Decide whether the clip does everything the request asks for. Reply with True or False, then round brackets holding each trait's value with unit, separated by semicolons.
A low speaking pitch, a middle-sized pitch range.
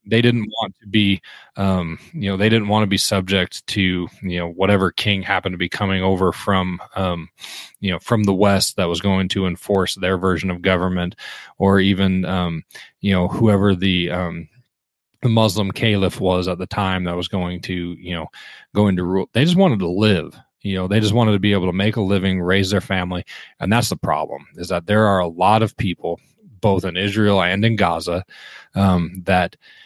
False (95 Hz; 2.1 semitones)